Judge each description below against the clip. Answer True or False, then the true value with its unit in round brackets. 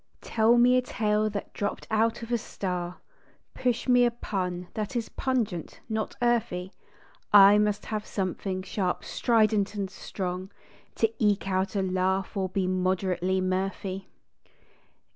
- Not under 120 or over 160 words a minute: True (145 wpm)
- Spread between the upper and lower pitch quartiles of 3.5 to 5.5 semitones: False (2.9 semitones)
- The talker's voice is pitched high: True (200 Hz)